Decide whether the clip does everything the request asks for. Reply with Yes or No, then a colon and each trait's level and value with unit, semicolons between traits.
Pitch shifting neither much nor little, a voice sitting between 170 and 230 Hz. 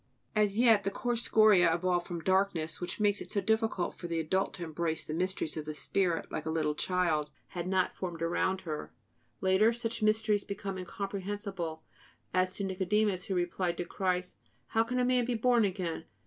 Yes: average, 3.4 semitones; medium, 185 Hz